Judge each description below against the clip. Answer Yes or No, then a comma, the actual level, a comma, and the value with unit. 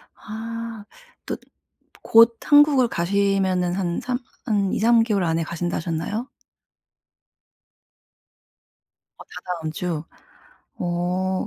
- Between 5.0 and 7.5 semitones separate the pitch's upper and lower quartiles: No, average, 4.6 semitones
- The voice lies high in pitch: Yes, high, 195 Hz